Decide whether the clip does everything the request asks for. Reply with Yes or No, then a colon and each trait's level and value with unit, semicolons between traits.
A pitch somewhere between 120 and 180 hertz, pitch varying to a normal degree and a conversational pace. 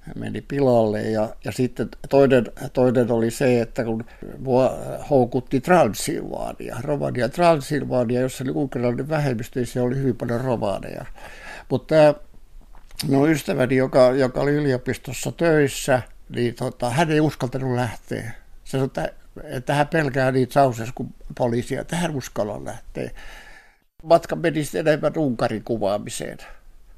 Yes: low, 130 Hz; average, 3.2 semitones; average, 125 wpm